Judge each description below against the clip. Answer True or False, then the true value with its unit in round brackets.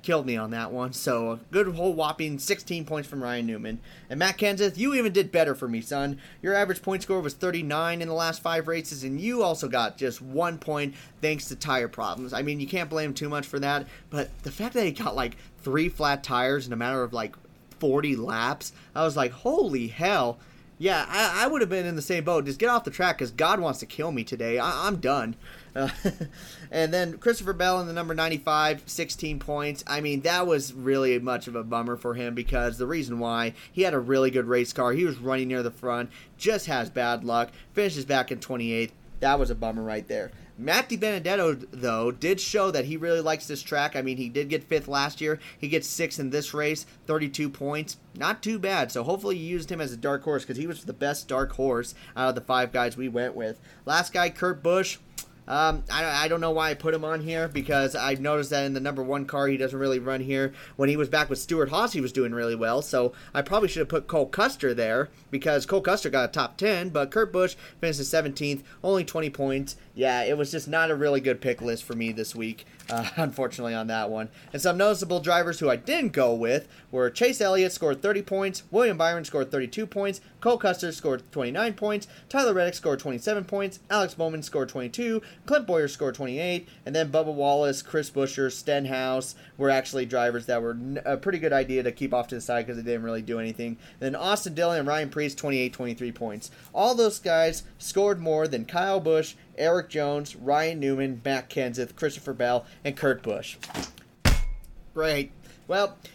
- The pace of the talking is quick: True (220 wpm)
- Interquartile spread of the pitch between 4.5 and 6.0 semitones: True (4.8 semitones)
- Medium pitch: True (145 Hz)